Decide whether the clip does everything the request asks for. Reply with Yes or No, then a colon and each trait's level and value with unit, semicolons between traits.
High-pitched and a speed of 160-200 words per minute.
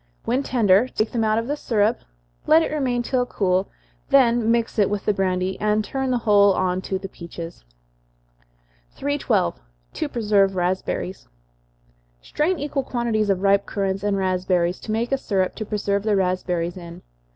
Yes: high, 205 Hz; average, 165 wpm